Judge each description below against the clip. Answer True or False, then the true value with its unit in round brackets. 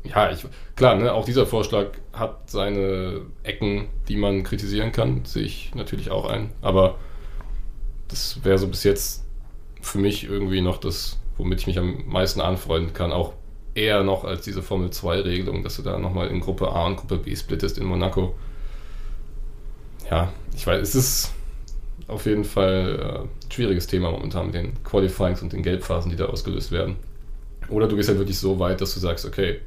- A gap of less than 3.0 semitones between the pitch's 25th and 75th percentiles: True (2.5 semitones)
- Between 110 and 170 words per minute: False (180 wpm)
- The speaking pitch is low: True (95 Hz)